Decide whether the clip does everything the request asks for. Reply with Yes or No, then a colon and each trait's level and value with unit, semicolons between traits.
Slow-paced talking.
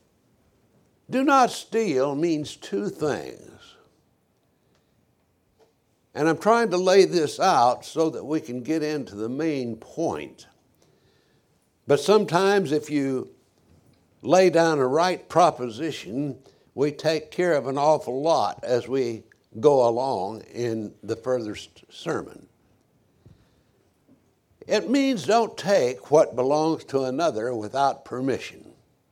Yes: slow, 115 wpm